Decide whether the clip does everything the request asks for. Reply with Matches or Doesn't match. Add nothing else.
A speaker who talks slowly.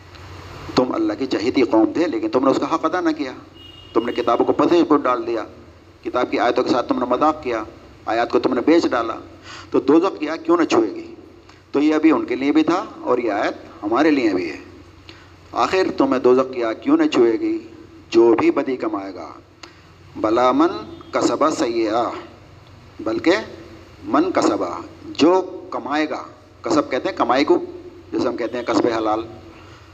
Doesn't match